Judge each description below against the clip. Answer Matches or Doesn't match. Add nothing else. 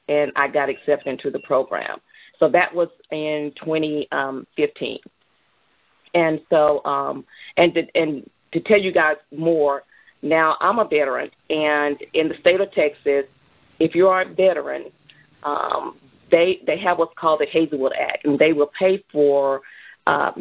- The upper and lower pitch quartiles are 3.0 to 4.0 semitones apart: Doesn't match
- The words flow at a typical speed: Matches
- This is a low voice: Doesn't match